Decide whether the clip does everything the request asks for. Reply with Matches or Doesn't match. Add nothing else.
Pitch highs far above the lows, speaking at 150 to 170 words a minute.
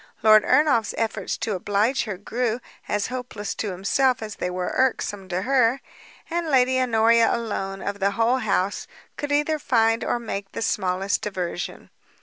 Doesn't match